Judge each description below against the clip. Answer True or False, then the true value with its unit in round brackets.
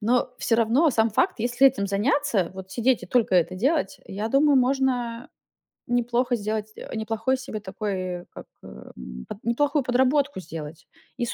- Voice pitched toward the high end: True (230 Hz)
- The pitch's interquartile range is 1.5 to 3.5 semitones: False (4.8 semitones)